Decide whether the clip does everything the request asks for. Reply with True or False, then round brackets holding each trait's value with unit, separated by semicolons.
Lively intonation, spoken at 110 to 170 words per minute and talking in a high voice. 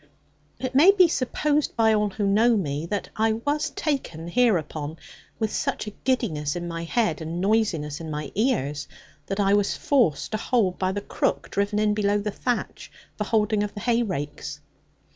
False (5.7 semitones; 180 wpm; 205 Hz)